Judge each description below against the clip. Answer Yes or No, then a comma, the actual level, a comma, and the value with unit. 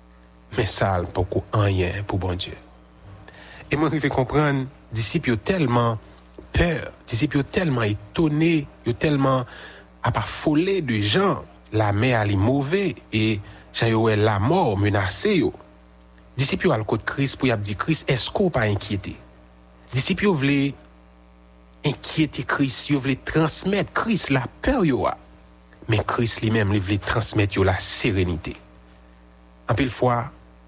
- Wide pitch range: Yes, wide, 7.9 semitones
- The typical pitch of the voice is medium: No, low, 110 Hz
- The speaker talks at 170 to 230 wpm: No, average, 160 wpm